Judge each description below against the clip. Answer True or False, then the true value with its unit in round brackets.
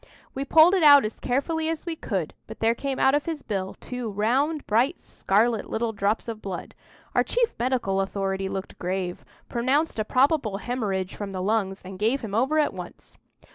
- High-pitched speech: True (230 Hz)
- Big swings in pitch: True (6.1 semitones)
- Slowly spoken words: False (190 wpm)